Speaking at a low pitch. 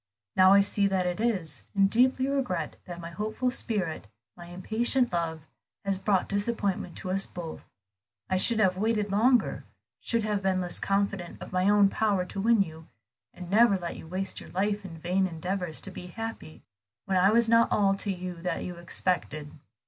No: high, 195 Hz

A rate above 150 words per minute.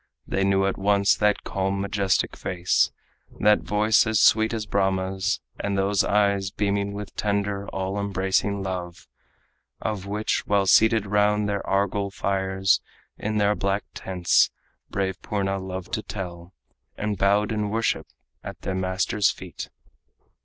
No: average, 140 wpm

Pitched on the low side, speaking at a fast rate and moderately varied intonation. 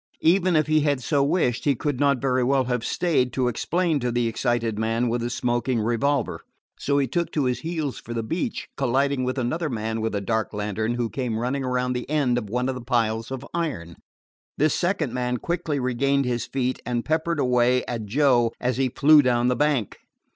Yes: low, 125 Hz; fast, 210 wpm; average, 3.1 semitones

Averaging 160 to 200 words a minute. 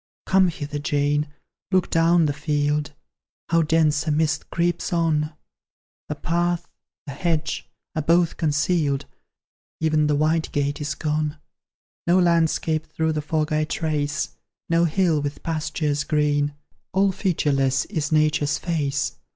No: slow, 135 wpm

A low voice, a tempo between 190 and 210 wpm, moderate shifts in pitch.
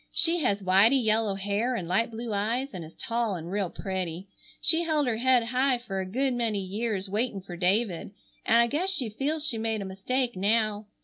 No: high, 220 Hz; fast, 205 wpm; average, 4.3 semitones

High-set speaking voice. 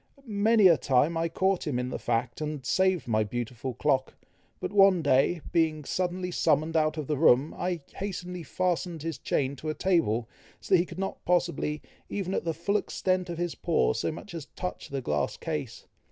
No: medium, 165 Hz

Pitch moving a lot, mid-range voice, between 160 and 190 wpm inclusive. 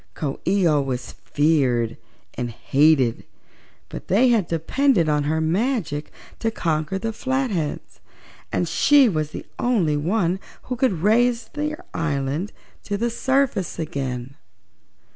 No: wide, 7.8 semitones; medium, 170 Hz; average, 145 wpm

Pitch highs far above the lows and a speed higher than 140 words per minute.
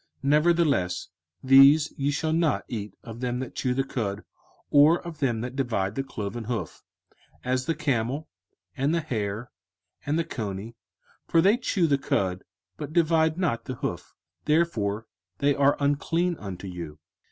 Yes: wide, 5.9 semitones; average, 160 wpm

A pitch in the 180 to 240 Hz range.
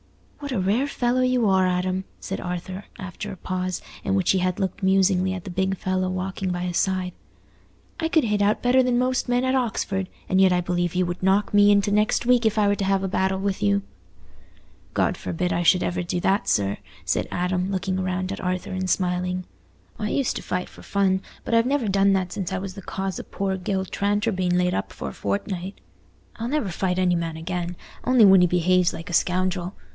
Yes: high, 190 Hz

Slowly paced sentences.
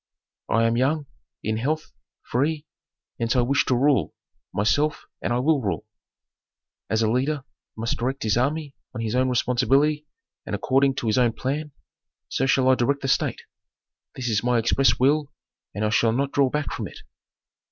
No: average, 175 wpm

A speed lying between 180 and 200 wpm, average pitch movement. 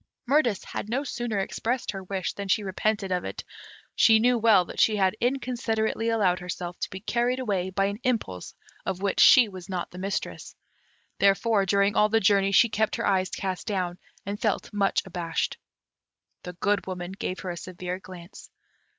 Yes: average, 185 wpm; average, 3.1 semitones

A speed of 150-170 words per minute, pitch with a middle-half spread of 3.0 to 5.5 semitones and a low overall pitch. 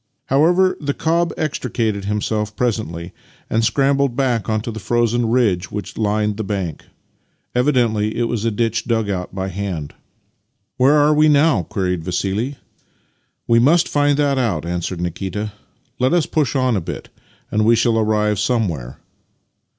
Yes: average, 165 wpm; average, 4.5 semitones; low, 115 Hz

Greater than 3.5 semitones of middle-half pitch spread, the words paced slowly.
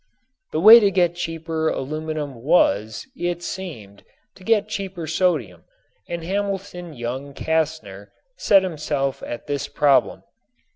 Yes: average, 5.0 semitones; slow, 125 wpm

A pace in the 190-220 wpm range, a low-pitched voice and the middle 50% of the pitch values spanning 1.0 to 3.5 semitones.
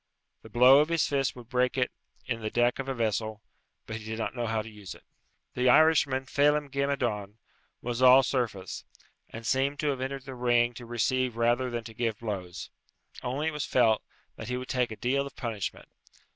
Yes: fast, 205 wpm; low, 125 Hz; average, 3.0 semitones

